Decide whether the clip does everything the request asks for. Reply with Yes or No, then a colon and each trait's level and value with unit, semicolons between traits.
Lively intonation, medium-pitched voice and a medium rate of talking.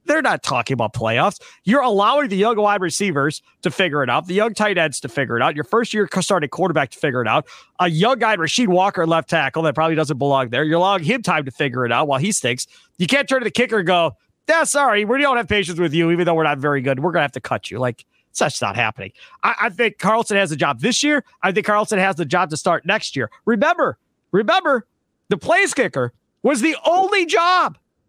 No: wide, 6.9 semitones; medium, 180 Hz; fast, 250 wpm